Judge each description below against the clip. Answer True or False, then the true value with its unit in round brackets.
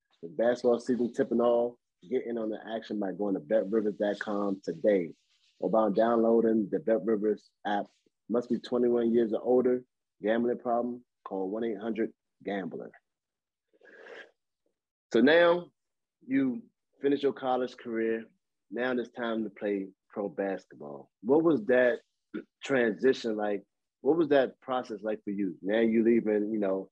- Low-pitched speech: True (115 Hz)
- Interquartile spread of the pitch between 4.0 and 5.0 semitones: False (2.8 semitones)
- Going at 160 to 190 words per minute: False (145 wpm)